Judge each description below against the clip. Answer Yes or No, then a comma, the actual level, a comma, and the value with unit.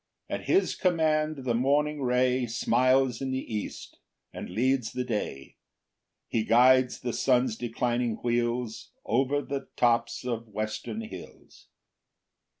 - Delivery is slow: Yes, slow, 130 wpm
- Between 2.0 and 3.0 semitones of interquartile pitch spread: Yes, narrow, 2.4 semitones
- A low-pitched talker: Yes, low, 125 Hz